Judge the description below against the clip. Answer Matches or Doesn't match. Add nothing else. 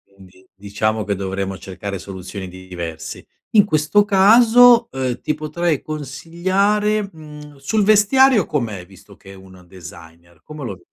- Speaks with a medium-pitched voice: Doesn't match